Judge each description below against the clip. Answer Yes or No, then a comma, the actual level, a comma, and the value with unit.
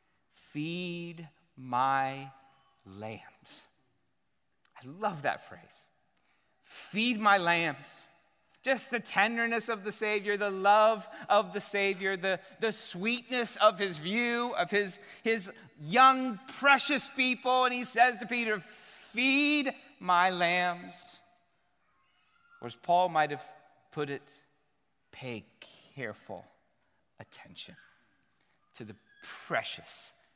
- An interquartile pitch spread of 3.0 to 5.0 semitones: No, wide, 5.6 semitones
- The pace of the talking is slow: Yes, slow, 105 wpm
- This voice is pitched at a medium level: No, high, 205 Hz